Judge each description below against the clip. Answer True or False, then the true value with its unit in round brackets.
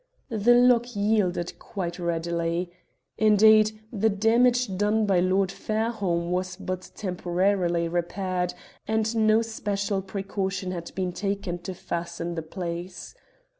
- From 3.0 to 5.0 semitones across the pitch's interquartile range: True (3.5 semitones)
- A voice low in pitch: False (190 Hz)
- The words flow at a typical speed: False (120 wpm)